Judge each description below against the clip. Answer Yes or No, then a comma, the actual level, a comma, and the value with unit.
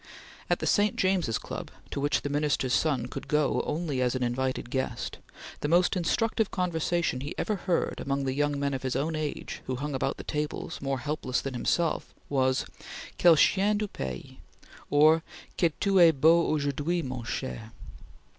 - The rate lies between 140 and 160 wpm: No, average, 175 wpm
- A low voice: No, medium, 145 Hz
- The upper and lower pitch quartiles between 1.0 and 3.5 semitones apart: No, average, 4.4 semitones